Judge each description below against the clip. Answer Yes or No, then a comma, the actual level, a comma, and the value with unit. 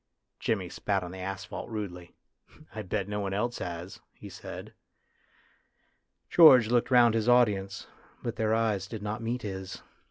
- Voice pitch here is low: Yes, low, 105 Hz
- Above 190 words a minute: No, average, 160 wpm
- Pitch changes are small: No, average, 3.2 semitones